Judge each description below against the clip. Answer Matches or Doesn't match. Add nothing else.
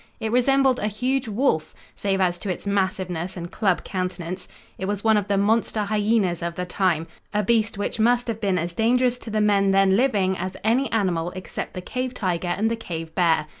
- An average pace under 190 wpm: Doesn't match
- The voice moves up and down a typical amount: Matches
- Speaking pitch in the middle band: Doesn't match